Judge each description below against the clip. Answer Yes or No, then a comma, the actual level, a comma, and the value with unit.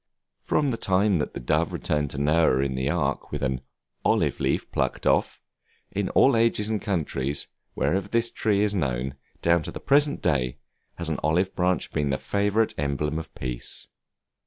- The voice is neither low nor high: No, very low, 85 Hz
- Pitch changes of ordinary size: No, wide, 6.7 semitones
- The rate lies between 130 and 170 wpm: No, average, 180 wpm